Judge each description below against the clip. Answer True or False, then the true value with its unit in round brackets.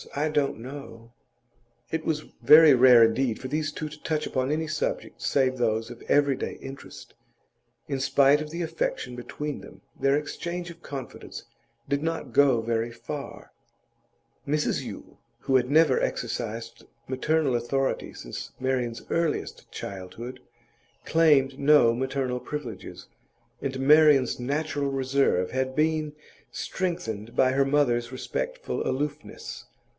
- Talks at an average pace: False (130 wpm)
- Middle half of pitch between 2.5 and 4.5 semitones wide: True (3.4 semitones)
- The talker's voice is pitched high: False (135 Hz)